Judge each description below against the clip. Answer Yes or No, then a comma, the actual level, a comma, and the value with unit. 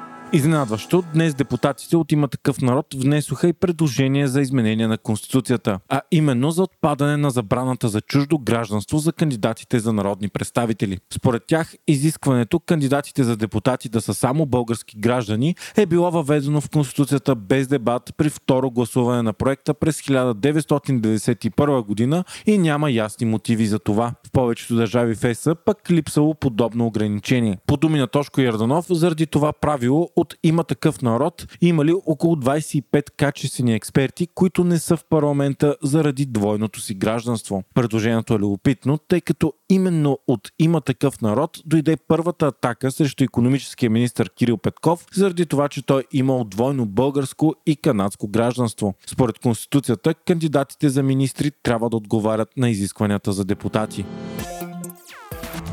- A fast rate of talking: No, average, 145 wpm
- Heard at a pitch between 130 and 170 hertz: Yes, low, 135 Hz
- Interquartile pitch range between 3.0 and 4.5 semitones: No, average, 5.0 semitones